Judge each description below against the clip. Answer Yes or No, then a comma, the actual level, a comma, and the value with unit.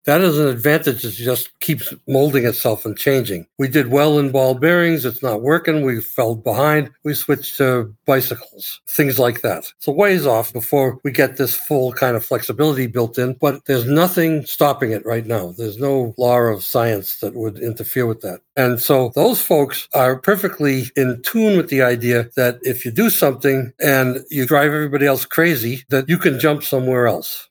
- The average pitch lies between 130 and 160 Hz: Yes, low, 135 Hz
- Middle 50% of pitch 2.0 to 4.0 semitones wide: Yes, average, 3.4 semitones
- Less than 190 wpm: No, average, 195 wpm